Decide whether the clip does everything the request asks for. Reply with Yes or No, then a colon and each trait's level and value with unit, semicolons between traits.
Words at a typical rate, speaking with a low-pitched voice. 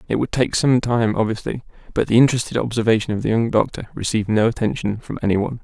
No: fast, 215 wpm; low, 115 Hz